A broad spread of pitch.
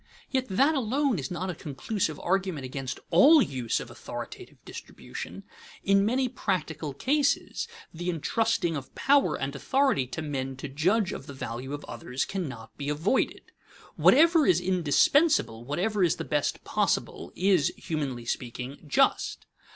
Yes: wide, 8.3 semitones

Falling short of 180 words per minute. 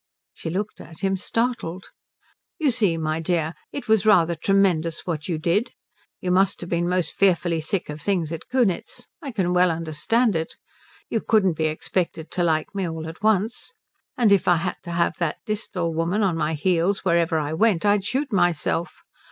No: average, 185 wpm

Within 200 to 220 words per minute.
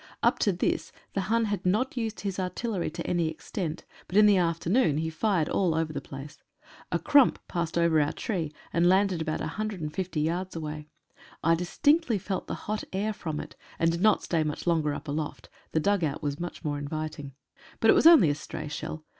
Yes: fast, 205 wpm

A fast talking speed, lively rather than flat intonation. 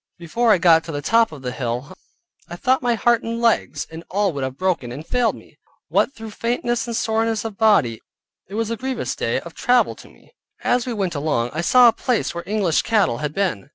Yes: fast, 225 wpm; wide, 6.6 semitones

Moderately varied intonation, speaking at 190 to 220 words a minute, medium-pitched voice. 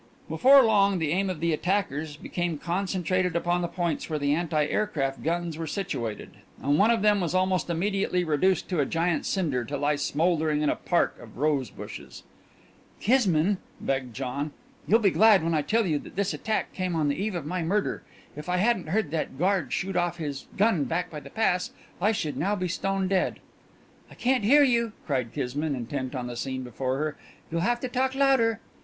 Yes: average, 4.9 semitones; fast, 205 wpm; medium, 175 Hz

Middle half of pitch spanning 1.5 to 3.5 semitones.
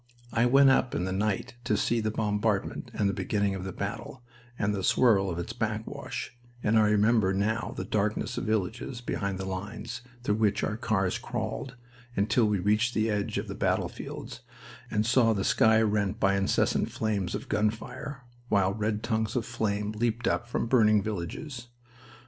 Yes: narrow, 2.4 semitones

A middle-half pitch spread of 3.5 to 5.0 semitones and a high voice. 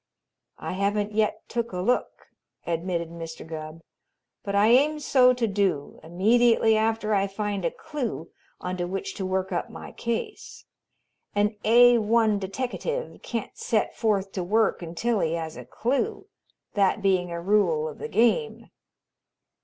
Yes: average, 4.5 semitones; high, 205 Hz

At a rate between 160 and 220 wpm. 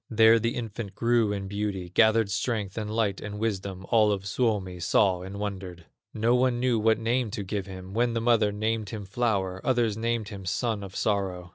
Yes: average, 195 wpm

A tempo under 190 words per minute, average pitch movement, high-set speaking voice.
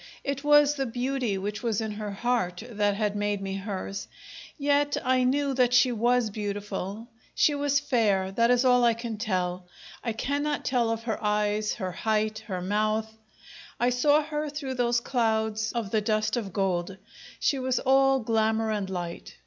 Yes: average, 175 wpm; average, 3.7 semitones; high, 225 Hz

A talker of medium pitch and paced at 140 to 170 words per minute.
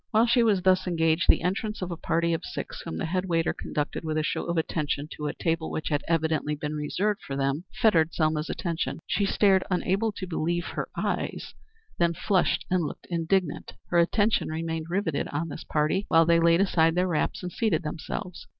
No: medium, 170 Hz; fast, 205 wpm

